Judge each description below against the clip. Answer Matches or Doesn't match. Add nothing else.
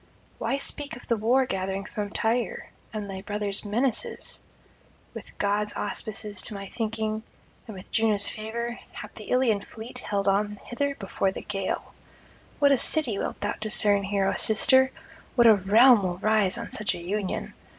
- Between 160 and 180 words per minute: Matches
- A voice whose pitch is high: Matches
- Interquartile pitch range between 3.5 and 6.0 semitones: Doesn't match